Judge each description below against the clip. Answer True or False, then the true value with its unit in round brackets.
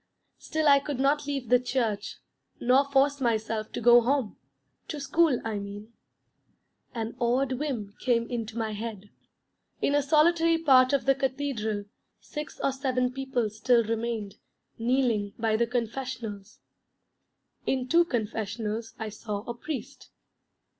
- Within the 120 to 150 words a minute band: True (140 wpm)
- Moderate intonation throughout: True (3.7 semitones)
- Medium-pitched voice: False (245 Hz)